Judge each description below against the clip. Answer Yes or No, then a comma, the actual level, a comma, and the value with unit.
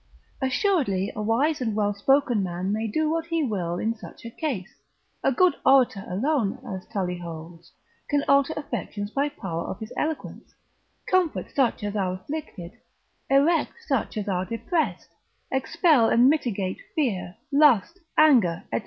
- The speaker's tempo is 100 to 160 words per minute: Yes, average, 155 wpm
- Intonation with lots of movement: Yes, wide, 7.3 semitones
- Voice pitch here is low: No, high, 230 Hz